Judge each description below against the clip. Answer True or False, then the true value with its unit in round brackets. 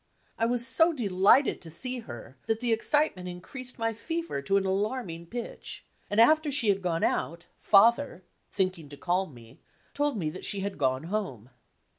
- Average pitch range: False (6.2 semitones)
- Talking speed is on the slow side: False (175 wpm)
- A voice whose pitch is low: False (200 Hz)